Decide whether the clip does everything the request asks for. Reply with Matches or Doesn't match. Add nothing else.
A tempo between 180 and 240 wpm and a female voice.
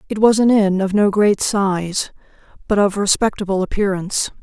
Doesn't match